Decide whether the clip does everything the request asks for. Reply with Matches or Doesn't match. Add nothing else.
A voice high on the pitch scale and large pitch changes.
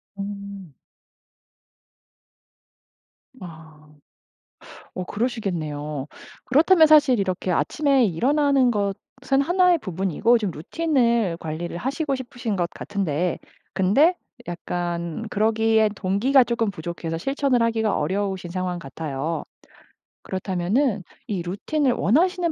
Matches